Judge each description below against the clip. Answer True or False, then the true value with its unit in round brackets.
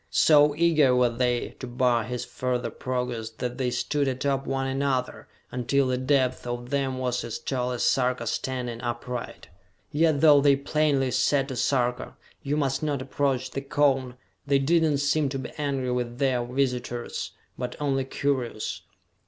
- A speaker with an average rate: True (165 wpm)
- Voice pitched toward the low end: True (130 Hz)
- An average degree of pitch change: False (2.2 semitones)